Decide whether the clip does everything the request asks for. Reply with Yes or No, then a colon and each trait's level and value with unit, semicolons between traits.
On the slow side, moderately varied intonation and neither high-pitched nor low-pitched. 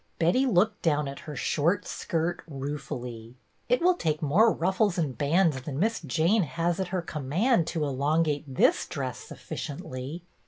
No: average, 165 wpm; average, 4.6 semitones; medium, 160 Hz